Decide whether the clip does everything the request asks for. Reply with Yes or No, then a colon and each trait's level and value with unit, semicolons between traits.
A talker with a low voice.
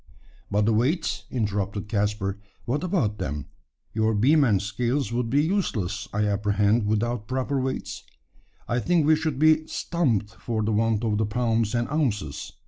Yes: low, 115 Hz